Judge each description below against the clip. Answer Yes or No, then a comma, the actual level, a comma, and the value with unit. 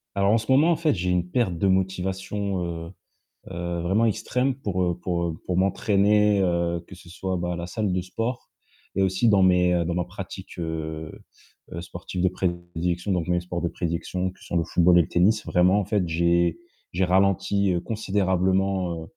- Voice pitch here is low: Yes, very low, 90 Hz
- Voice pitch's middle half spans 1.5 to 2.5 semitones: Yes, narrow, 2.1 semitones